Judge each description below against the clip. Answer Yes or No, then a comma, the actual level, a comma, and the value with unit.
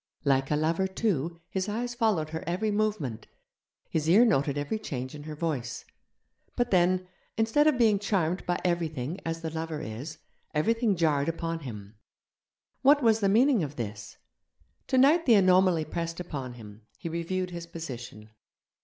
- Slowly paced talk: No, average, 160 wpm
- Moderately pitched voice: Yes, medium, 170 Hz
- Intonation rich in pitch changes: Yes, wide, 6.0 semitones